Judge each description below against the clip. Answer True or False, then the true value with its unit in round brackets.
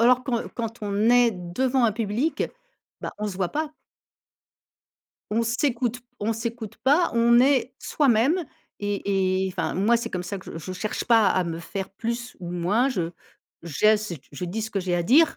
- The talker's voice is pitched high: True (220 Hz)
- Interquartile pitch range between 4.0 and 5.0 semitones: True (4.3 semitones)